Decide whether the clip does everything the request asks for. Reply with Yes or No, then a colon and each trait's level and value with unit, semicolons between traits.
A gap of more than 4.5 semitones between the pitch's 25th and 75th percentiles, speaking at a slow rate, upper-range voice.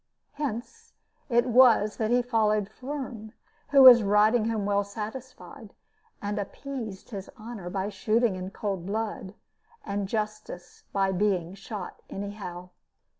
No: average, 3.1 semitones; slow, 125 wpm; high, 210 Hz